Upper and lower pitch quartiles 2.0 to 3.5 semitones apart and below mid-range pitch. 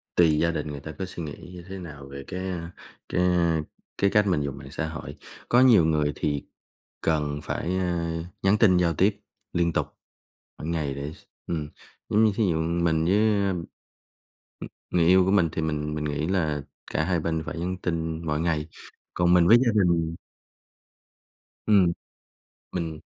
Yes: average, 2.8 semitones; very low, 85 Hz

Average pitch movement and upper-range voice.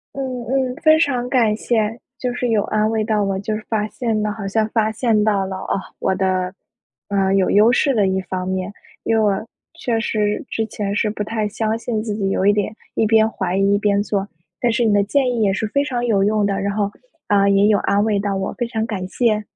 No: narrow, 2.2 semitones; high, 210 Hz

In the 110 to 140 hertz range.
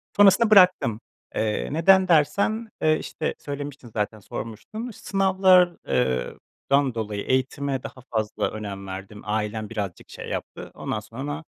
Yes: low, 135 Hz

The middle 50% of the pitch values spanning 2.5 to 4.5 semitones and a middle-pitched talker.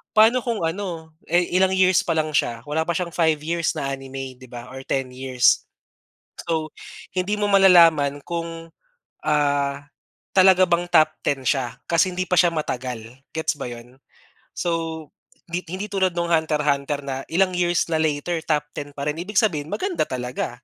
Yes: average, 4.0 semitones; medium, 160 Hz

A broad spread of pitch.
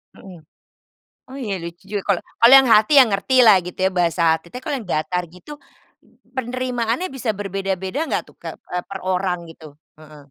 Yes: wide, 5.8 semitones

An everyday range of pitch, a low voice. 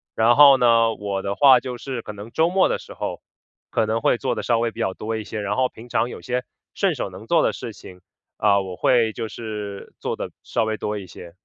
Yes: average, 3.3 semitones; low, 115 Hz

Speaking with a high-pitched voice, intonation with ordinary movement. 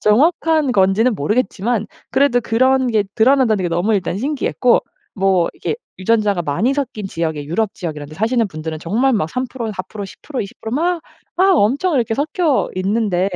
No: high, 220 Hz; wide, 5.7 semitones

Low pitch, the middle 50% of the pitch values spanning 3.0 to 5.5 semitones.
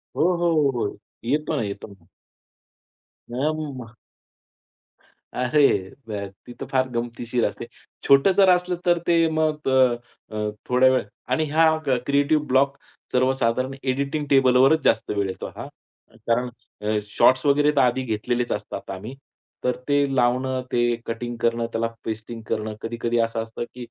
Yes: low, 125 Hz; average, 3.5 semitones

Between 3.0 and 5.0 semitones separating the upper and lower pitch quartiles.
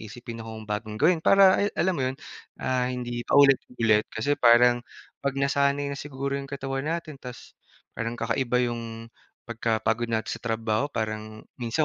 Yes: average, 3.5 semitones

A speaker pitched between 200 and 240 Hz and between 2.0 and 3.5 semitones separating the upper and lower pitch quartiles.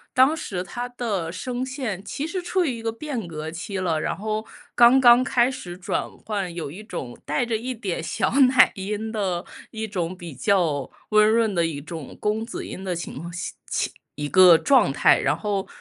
No: high, 210 Hz; wide, 5.6 semitones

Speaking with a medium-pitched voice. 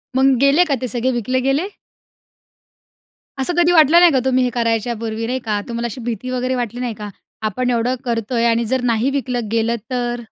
No: high, 245 Hz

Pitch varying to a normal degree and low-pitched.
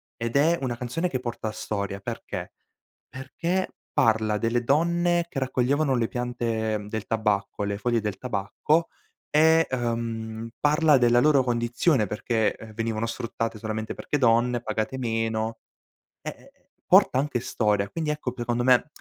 Yes: average, 3.5 semitones; low, 120 Hz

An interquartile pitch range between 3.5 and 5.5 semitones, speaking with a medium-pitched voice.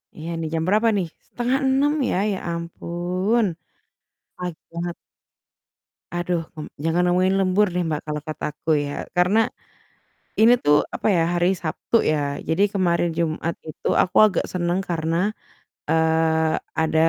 No: narrow, 2.6 semitones; medium, 175 Hz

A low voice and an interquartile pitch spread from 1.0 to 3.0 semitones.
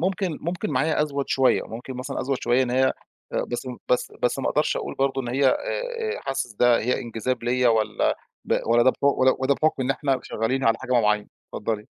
Yes: low, 130 Hz; average, 2.7 semitones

